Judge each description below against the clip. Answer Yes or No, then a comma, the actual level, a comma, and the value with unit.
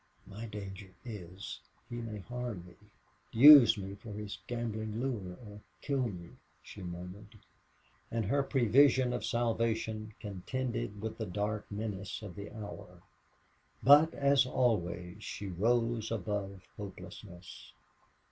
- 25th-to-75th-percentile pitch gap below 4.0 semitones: Yes, average, 3.2 semitones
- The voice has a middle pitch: No, low, 105 Hz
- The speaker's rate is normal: No, slow, 125 wpm